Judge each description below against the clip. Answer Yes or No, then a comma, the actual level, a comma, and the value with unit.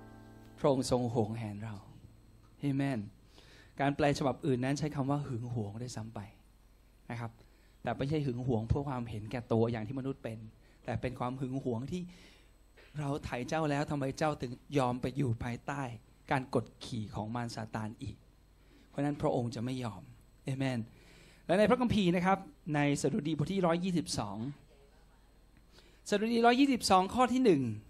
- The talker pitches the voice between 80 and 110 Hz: No, low, 130 Hz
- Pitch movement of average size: Yes, average, 4.3 semitones